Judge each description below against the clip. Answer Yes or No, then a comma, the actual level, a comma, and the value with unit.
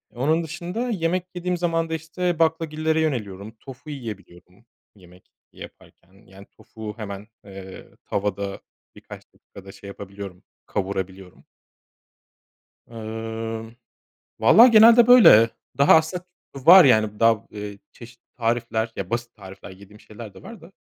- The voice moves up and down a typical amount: No, wide, 8.2 semitones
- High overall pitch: No, low, 115 Hz